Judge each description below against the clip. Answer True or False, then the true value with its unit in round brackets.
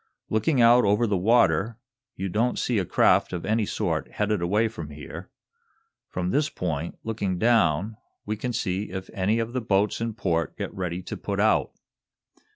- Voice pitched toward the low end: True (105 Hz)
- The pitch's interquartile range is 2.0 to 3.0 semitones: False (4.0 semitones)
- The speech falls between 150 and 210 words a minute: True (175 wpm)